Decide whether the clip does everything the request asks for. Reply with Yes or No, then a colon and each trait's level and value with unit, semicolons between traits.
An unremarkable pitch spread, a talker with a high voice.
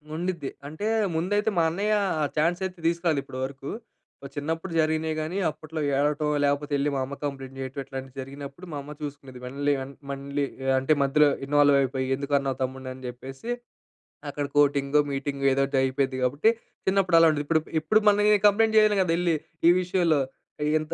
No: average, 3.4 semitones; medium, 145 Hz